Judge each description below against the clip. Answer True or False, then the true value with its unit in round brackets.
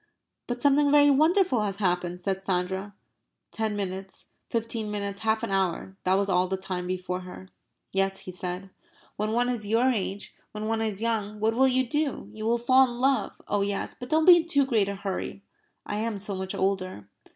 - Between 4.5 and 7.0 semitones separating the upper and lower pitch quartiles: False (4.1 semitones)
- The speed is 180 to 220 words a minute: True (200 wpm)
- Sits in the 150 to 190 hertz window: False (210 Hz)